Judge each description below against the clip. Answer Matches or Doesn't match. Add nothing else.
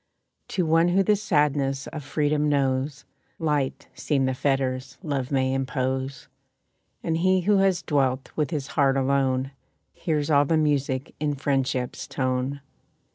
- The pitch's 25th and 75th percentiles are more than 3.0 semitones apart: Doesn't match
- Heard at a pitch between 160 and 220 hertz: Doesn't match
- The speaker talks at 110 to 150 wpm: Matches